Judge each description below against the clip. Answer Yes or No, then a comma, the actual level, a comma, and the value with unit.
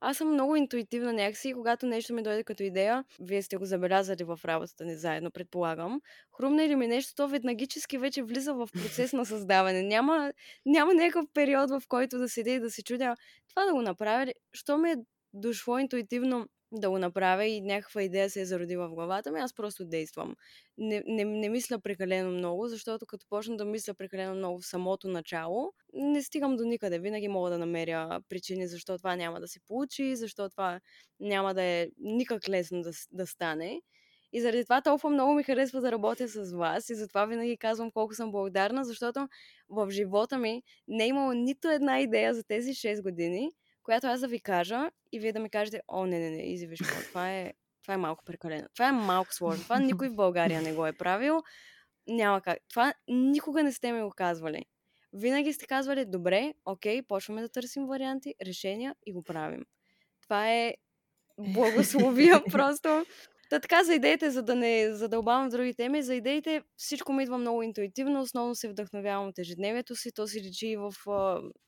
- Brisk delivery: Yes, fast, 195 wpm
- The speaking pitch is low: No, high, 225 Hz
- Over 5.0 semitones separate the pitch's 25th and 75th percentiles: Yes, wide, 5.4 semitones